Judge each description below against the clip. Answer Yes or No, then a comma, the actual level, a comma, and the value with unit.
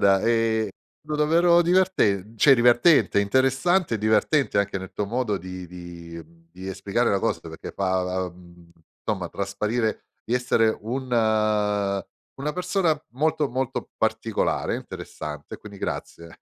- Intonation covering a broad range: Yes, wide, 6.1 semitones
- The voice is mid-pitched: No, low, 110 Hz